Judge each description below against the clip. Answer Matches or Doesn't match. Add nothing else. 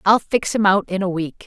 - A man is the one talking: Doesn't match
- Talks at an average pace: Doesn't match